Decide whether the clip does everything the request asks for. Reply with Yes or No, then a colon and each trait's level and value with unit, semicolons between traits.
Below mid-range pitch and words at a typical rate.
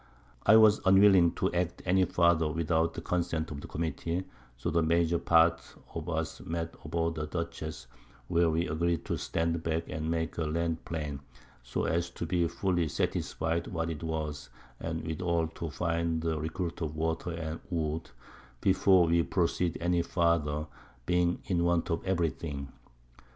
Yes: very low, 85 Hz; average, 165 wpm